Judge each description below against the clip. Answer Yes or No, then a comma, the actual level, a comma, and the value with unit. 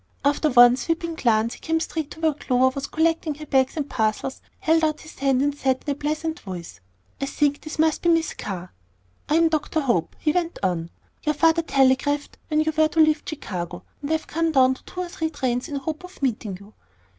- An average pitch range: Yes, average, 3.6 semitones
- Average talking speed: No, fast, 225 wpm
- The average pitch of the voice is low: No, very high, 290 Hz